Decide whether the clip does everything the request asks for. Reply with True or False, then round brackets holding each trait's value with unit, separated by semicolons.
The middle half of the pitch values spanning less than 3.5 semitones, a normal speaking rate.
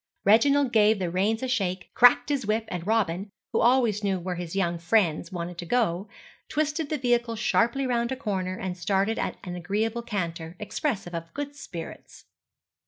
False (5.1 semitones; 175 wpm)